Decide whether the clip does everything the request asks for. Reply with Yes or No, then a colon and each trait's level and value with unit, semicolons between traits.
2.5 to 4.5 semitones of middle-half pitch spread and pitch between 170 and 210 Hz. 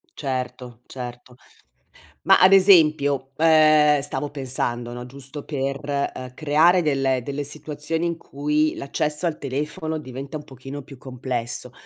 No: average, 2.8 semitones; medium, 140 Hz